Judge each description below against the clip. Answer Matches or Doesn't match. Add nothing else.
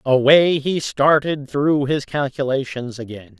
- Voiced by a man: Matches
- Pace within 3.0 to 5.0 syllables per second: Matches